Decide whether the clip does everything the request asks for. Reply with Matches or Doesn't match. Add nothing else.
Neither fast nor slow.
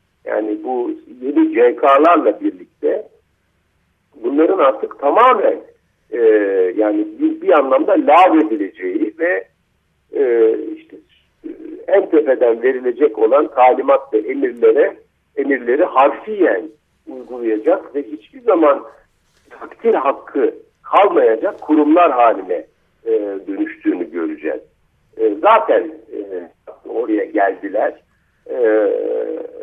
Doesn't match